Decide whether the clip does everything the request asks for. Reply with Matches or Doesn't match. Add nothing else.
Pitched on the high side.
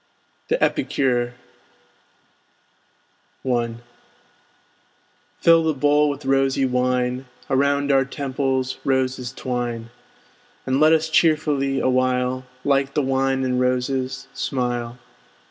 Doesn't match